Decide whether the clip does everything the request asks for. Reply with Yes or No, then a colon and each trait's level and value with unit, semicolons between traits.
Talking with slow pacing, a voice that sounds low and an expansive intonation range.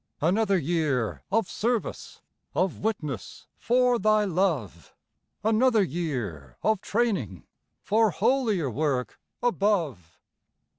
No: slow, 95 wpm; medium, 185 Hz; wide, 8.2 semitones